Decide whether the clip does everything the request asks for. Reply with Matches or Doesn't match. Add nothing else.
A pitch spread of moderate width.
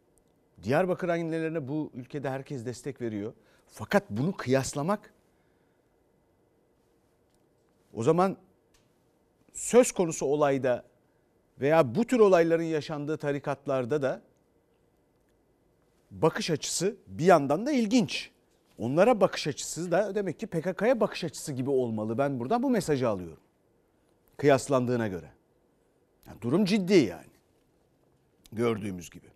Doesn't match